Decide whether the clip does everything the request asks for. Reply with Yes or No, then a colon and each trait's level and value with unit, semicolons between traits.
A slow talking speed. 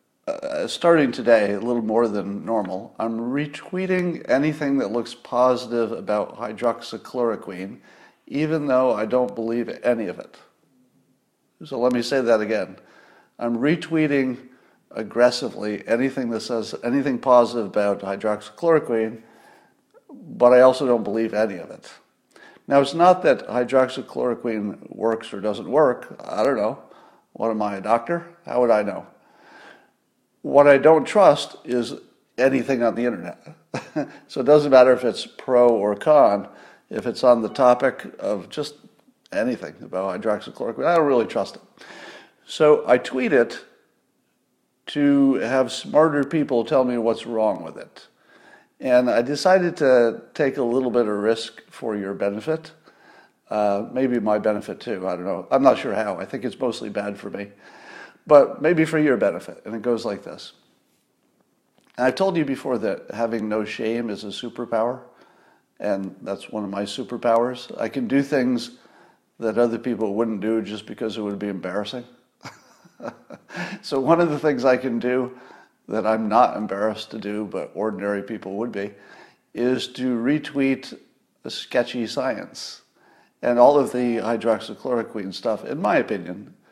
No: average, 155 wpm